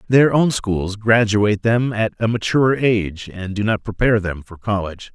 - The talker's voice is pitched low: Yes, low, 105 Hz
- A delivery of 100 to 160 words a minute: No, average, 185 wpm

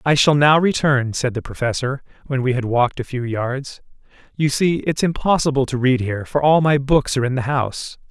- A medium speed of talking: No, fast, 215 wpm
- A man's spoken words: Yes, male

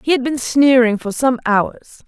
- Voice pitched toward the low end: No, very high, 250 Hz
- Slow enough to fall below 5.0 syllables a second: Yes, 4.3 syllables/s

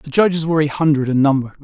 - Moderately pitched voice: Yes, medium, 150 Hz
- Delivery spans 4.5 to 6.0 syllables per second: No, 7.1 syllables/s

